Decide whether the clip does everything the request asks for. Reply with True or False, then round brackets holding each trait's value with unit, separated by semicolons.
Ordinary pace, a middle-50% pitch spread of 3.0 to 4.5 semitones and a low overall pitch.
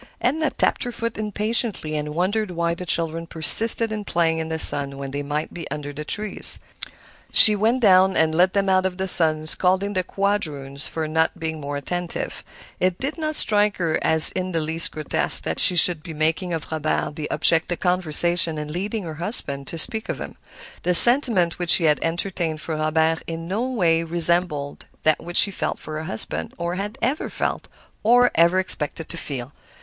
False (195 wpm; 3.8 semitones; 170 Hz)